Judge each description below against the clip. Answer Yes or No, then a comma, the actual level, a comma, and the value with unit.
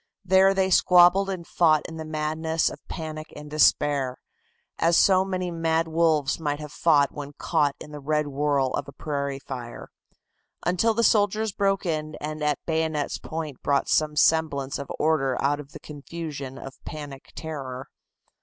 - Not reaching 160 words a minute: No, average, 170 wpm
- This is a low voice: No, medium, 155 Hz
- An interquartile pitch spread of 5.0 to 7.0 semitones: No, average, 2.7 semitones